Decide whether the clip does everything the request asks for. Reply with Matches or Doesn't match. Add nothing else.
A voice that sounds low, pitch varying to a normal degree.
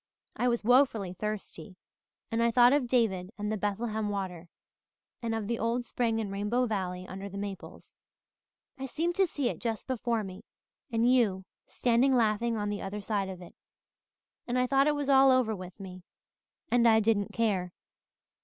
Doesn't match